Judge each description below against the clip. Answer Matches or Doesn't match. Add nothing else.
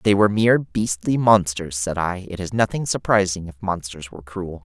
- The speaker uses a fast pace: Doesn't match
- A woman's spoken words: Doesn't match